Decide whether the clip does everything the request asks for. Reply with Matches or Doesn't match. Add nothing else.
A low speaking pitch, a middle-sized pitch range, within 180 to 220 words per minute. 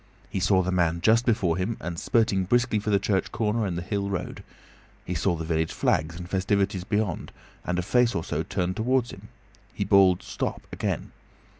Matches